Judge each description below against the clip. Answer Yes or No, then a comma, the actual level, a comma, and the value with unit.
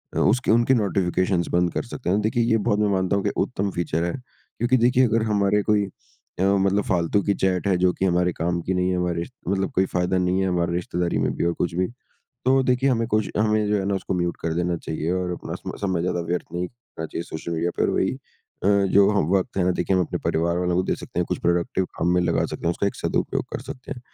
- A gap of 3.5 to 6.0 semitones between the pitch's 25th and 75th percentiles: No, average, 3.0 semitones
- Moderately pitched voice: No, very low, 95 Hz